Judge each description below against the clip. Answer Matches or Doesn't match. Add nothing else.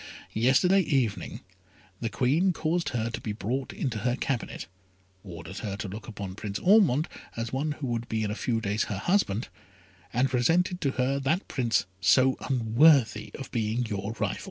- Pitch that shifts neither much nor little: Matches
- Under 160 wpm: Doesn't match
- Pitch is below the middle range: Matches